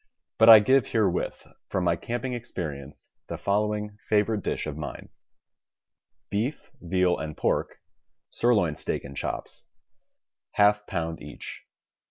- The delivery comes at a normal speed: No, slow, 130 wpm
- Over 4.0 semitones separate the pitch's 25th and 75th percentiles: Yes, average, 4.9 semitones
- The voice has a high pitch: No, low, 100 Hz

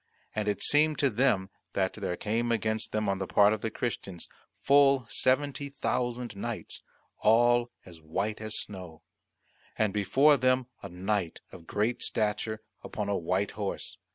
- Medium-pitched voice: No, low, 110 Hz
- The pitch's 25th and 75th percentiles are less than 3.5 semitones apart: No, average, 3.8 semitones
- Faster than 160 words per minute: No, average, 155 wpm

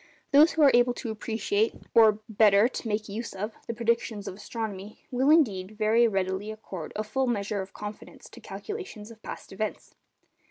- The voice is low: No, high, 215 Hz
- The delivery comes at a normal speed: Yes, average, 175 wpm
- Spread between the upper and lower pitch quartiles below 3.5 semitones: Yes, narrow, 2.5 semitones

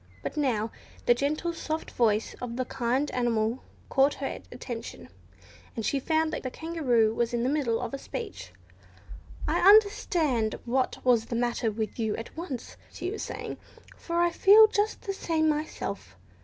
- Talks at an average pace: Yes, average, 165 wpm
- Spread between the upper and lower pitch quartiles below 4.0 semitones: No, wide, 5.6 semitones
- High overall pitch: Yes, very high, 260 Hz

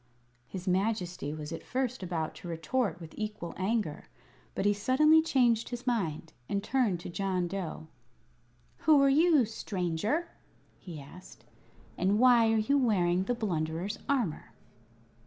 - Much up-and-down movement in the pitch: Yes, wide, 6.0 semitones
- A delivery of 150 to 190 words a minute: No, average, 140 wpm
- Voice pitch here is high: Yes, high, 200 Hz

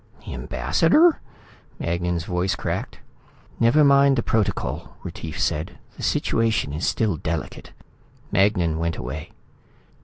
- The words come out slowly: Yes, slow, 115 wpm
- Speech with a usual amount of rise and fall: No, wide, 6.2 semitones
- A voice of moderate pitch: No, very low, 90 Hz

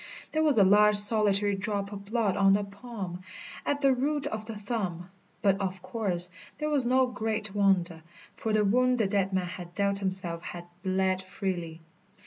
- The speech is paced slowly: No, average, 180 wpm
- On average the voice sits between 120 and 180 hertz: No, high, 200 Hz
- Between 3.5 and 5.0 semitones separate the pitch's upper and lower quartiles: No, average, 3.0 semitones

